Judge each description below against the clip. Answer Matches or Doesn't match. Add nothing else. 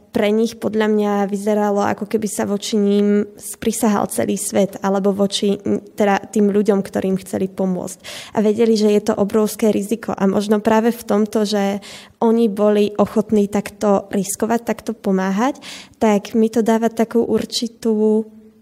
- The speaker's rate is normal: Matches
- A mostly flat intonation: Matches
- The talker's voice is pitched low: Doesn't match